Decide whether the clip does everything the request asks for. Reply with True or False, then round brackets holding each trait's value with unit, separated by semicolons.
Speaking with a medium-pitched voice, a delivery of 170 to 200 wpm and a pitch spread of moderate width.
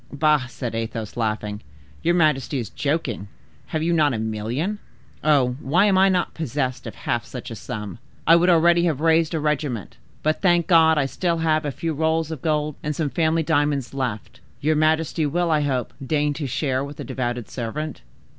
True (150 Hz; 195 wpm; 4.0 semitones)